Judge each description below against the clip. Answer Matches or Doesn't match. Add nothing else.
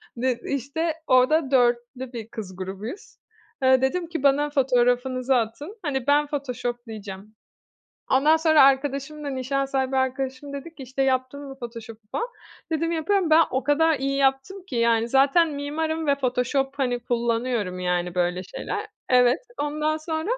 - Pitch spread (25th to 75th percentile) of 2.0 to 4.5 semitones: Matches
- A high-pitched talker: Matches